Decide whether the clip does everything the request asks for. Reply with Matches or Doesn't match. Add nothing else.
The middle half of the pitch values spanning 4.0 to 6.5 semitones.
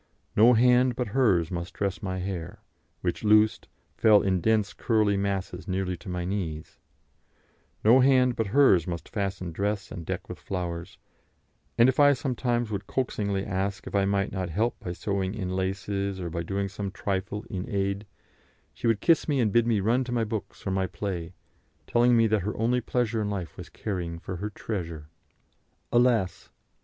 Doesn't match